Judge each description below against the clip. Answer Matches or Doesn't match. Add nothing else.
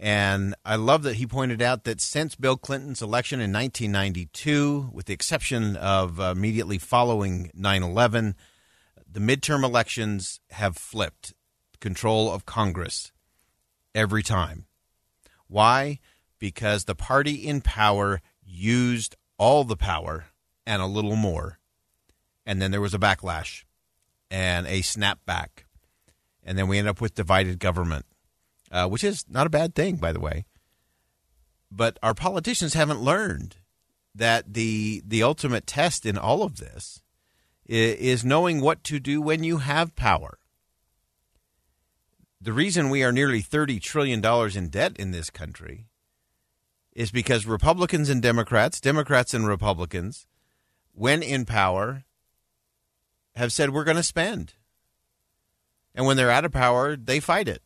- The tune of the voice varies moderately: Doesn't match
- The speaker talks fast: Doesn't match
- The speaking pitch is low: Matches